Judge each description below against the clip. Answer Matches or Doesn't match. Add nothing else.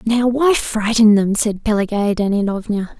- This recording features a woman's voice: Matches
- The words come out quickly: Doesn't match